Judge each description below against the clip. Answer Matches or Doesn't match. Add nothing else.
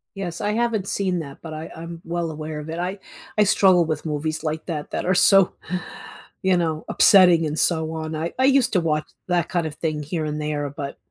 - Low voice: Doesn't match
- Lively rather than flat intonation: Doesn't match